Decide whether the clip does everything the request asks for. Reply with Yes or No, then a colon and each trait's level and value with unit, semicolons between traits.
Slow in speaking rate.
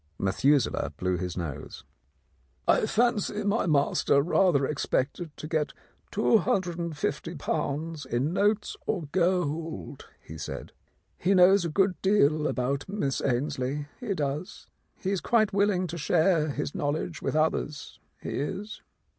Yes: slow, 130 wpm